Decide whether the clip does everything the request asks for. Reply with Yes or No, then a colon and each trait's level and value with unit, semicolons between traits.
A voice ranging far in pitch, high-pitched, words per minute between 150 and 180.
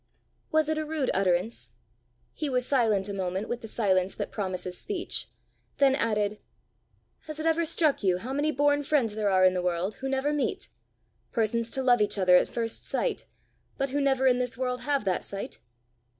No: wide, 6.3 semitones; high, 240 Hz; average, 195 wpm